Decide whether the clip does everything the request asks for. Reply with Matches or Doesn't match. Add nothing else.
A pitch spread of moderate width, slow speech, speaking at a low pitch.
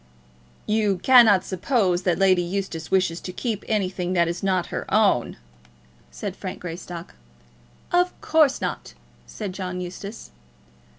Doesn't match